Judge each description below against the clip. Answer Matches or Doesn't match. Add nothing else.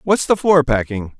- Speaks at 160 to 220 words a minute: Matches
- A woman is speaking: Doesn't match